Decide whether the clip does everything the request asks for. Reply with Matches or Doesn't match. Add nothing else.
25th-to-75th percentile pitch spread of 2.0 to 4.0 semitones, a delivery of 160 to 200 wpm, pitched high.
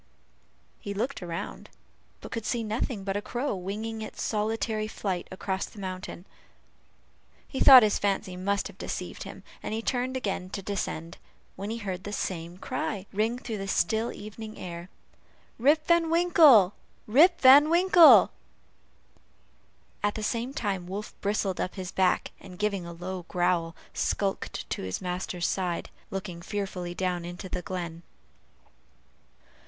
Doesn't match